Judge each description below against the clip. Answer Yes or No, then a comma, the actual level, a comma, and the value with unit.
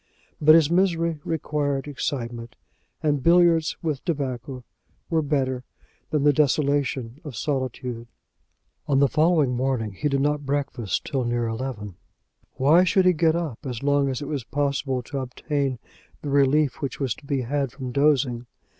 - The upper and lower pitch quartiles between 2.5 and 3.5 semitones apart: Yes, average, 2.9 semitones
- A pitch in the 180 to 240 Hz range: No, medium, 140 Hz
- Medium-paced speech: Yes, average, 155 wpm